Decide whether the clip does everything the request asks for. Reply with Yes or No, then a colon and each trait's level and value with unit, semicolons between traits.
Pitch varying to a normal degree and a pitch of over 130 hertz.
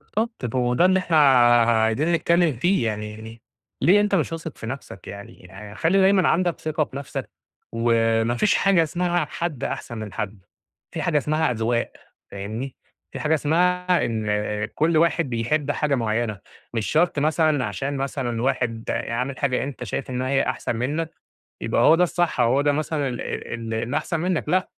No: wide, 6.1 semitones; medium, 140 Hz